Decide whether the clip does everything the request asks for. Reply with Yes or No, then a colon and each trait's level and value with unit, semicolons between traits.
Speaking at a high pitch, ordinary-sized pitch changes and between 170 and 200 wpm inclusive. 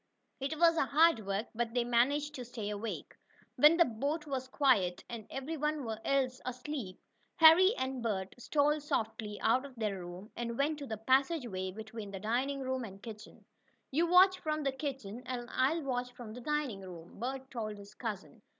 Yes: very high, 250 Hz; average, 4.8 semitones; average, 180 wpm